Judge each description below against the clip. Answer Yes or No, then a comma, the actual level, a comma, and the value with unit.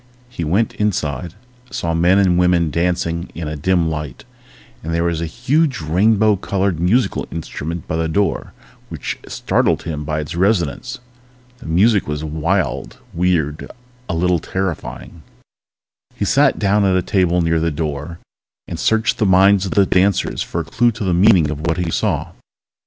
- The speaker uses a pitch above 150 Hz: No, very low, 85 Hz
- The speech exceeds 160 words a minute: Yes, average, 170 wpm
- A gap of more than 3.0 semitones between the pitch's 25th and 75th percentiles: Yes, average, 3.4 semitones